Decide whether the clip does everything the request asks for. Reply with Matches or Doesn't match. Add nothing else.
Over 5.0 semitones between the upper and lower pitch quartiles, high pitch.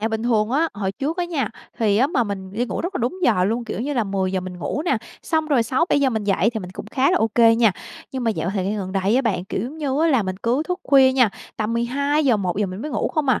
Matches